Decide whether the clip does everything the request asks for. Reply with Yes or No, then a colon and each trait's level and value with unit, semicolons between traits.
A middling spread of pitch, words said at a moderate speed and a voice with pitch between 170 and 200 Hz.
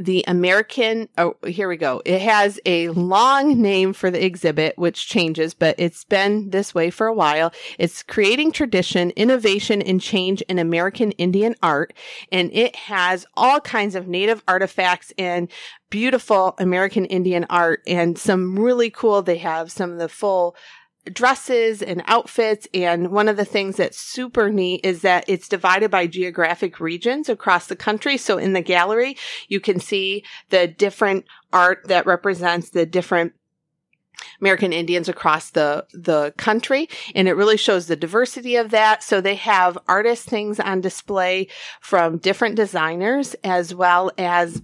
Yes: average, 3.4 semitones; average, 160 wpm; high, 190 Hz